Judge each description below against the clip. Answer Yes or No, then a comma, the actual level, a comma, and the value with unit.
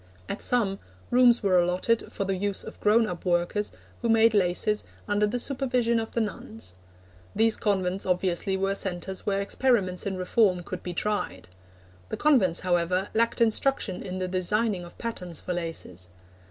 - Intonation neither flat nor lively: Yes, average, 3.8 semitones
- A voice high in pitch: Yes, high, 195 Hz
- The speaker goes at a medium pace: Yes, average, 165 wpm